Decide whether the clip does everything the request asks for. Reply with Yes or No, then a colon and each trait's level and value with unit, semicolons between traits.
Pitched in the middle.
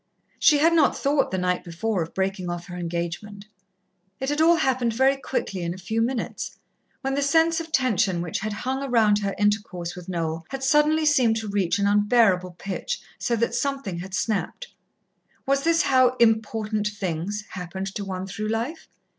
No: high, 215 Hz